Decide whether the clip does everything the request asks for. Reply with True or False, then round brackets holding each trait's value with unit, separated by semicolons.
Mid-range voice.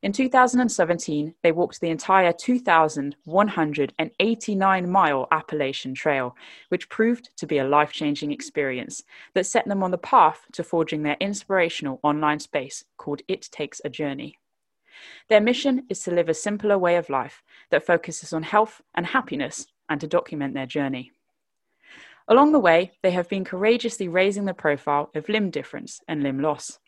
True (170 Hz)